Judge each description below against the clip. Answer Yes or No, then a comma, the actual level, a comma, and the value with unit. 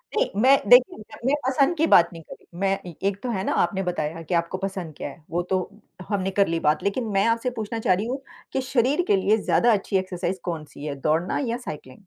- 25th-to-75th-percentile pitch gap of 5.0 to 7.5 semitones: Yes, wide, 5.6 semitones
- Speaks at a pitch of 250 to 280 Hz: No, high, 195 Hz